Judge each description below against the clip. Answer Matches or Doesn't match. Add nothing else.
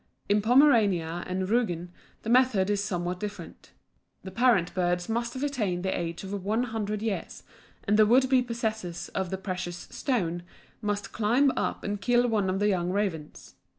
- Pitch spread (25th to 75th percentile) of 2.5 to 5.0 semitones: Matches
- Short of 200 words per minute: Matches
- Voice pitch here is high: Matches